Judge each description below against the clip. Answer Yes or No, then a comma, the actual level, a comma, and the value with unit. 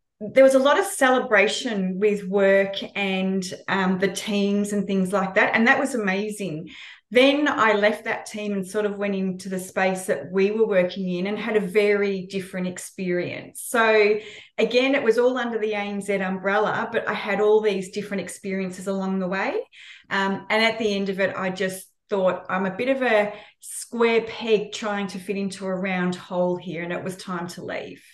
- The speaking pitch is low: No, high, 200 Hz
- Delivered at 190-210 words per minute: Yes, average, 200 wpm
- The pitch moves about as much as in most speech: No, narrow, 2.2 semitones